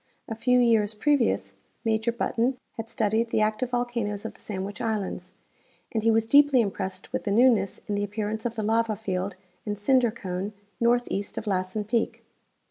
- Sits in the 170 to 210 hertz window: No, high, 220 Hz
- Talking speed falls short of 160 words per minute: No, average, 190 wpm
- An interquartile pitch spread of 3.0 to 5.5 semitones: No, narrow, 2.4 semitones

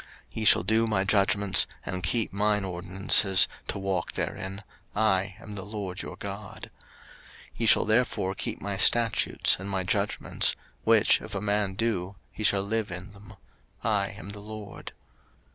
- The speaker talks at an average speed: Yes, average, 165 wpm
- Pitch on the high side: No, low, 100 Hz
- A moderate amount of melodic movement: No, narrow, 1.8 semitones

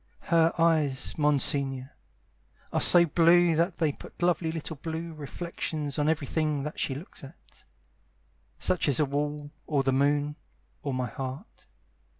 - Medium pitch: Yes, medium, 150 Hz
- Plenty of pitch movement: No, average, 2.8 semitones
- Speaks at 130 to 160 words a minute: Yes, average, 145 wpm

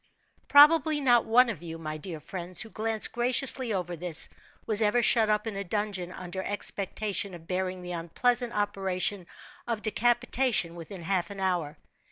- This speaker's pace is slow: No, average, 165 wpm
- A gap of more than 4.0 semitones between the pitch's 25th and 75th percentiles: Yes, average, 4.6 semitones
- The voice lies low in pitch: No, high, 200 Hz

